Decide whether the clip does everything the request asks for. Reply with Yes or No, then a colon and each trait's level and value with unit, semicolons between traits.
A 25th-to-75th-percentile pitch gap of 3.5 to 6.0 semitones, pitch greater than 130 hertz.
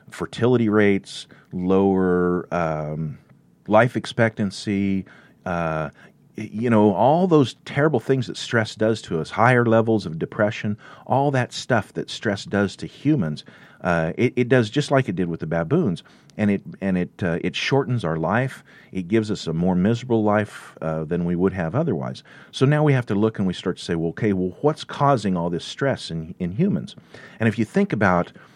No: average, 5.3 semitones; low, 105 Hz